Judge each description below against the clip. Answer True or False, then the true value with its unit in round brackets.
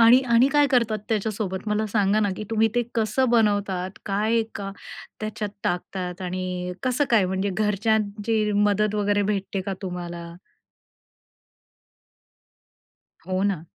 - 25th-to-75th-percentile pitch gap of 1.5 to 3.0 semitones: True (2.6 semitones)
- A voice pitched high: True (205 Hz)